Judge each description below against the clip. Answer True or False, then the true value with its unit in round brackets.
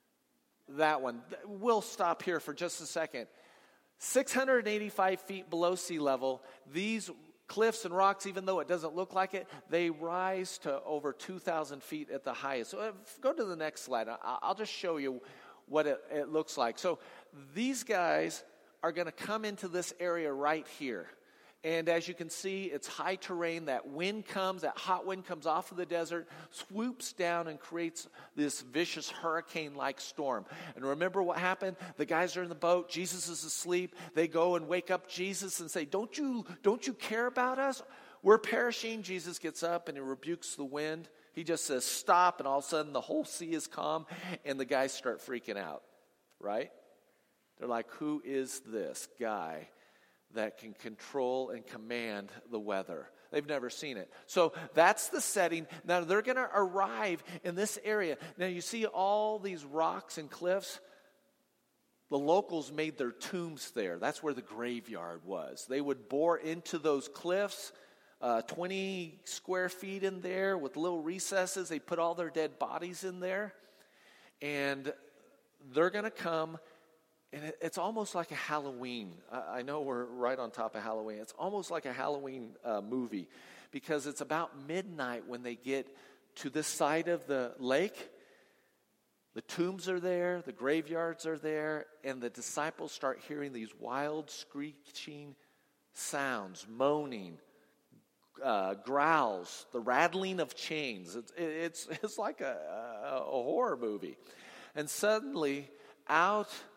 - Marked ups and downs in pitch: False (4.4 semitones)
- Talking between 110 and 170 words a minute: True (165 wpm)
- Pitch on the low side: False (165 Hz)